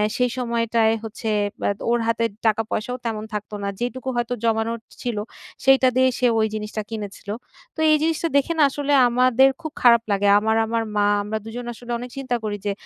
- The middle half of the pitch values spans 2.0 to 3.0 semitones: Yes, narrow, 2.5 semitones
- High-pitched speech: Yes, high, 235 Hz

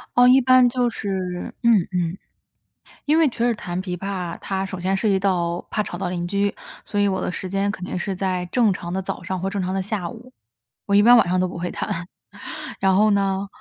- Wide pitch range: No, average, 2.7 semitones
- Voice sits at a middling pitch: No, high, 195 Hz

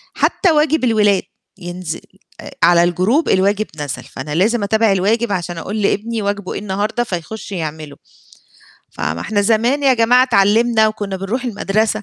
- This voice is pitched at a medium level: No, high, 205 Hz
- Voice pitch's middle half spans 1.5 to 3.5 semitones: No, average, 3.9 semitones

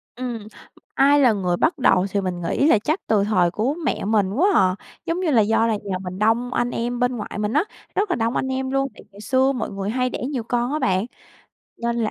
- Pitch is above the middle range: Yes, high, 230 Hz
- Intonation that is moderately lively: Yes, average, 4.4 semitones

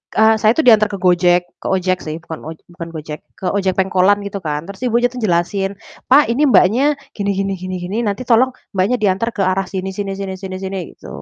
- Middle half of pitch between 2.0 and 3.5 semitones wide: Yes, average, 2.8 semitones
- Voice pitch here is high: Yes, high, 195 Hz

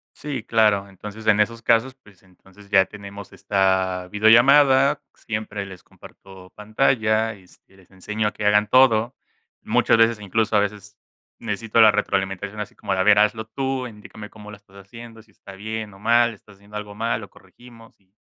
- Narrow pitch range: Yes, narrow, 2.3 semitones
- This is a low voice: Yes, low, 105 Hz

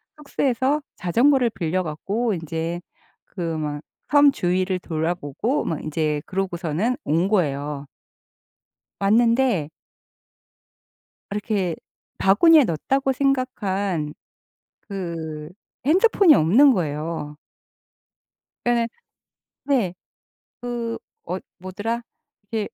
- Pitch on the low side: No, high, 190 Hz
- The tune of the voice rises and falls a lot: Yes, wide, 6.9 semitones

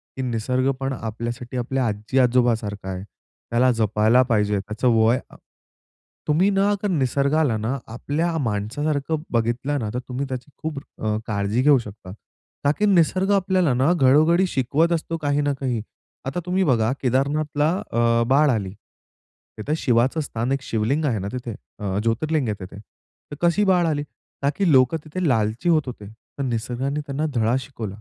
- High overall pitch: No, low, 130 Hz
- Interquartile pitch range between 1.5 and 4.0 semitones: No, average, 4.8 semitones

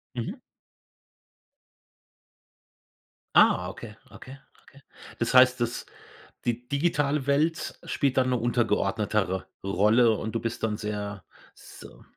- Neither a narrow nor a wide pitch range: Yes, average, 3.7 semitones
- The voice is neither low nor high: No, low, 120 Hz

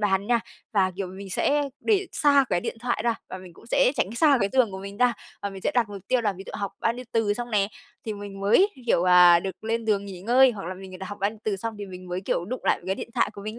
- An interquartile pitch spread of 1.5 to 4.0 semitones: Yes, average, 3.7 semitones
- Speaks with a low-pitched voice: No, high, 205 Hz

